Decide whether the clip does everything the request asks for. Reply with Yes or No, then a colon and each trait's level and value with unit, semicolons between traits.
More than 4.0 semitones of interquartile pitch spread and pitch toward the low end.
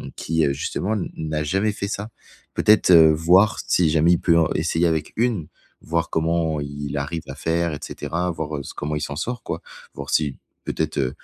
No: average, 2.8 semitones; very low, 80 Hz